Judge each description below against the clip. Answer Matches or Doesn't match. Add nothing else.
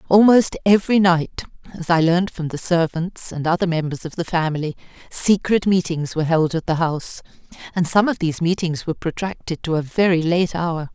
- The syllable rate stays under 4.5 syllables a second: Doesn't match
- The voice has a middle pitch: Matches